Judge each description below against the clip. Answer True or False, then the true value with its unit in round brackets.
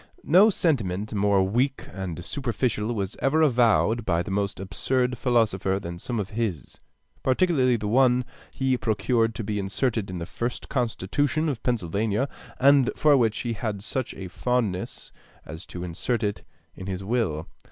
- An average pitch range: True (4.7 semitones)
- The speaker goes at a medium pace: True (160 wpm)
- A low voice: True (110 Hz)